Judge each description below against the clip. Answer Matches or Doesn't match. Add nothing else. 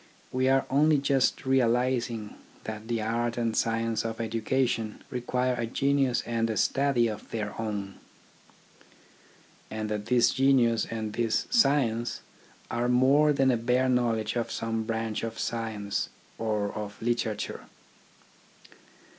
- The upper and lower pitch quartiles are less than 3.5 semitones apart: Matches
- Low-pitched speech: Matches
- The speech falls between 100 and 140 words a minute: Matches